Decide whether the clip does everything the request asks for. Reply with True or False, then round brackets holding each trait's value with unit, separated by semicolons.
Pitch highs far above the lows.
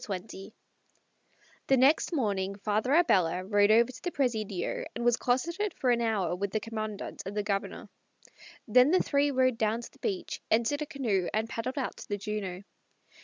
False (4.1 semitones)